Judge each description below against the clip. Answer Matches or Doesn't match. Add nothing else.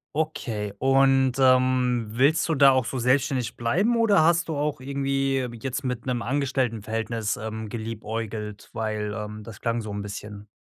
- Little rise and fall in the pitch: Doesn't match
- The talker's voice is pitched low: Matches